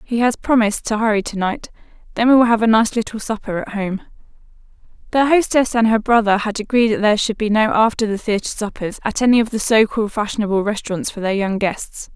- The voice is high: Yes, high, 220 Hz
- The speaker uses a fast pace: Yes, fast, 210 wpm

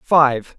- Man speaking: Yes, male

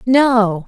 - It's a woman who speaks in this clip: Yes, female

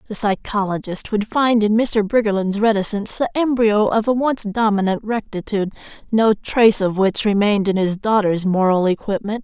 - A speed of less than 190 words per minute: Yes, average, 160 wpm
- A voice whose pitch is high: Yes, high, 210 Hz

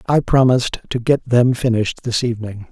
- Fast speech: No, average, 175 wpm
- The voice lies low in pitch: Yes, low, 120 Hz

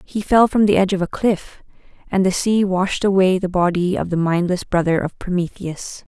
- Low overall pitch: No, medium, 185 Hz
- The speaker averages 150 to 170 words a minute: No, fast, 205 wpm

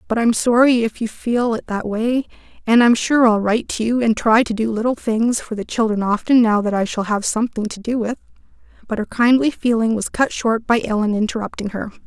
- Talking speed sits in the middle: No, fast, 230 wpm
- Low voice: No, high, 225 Hz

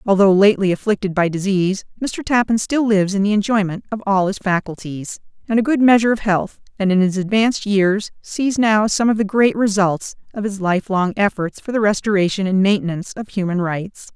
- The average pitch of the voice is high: Yes, high, 200 Hz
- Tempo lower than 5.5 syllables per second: No, 5.6 syllables/s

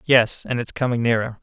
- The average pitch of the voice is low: Yes, low, 120 Hz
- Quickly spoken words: Yes, fast, 210 wpm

